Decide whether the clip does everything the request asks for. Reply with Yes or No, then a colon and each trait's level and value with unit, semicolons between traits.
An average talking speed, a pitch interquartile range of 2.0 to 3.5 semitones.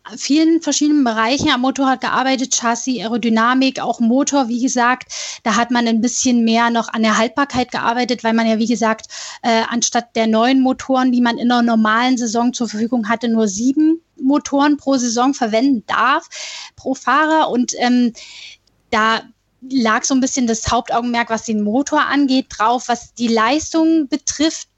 Yes: average, 170 wpm; narrow, 2.6 semitones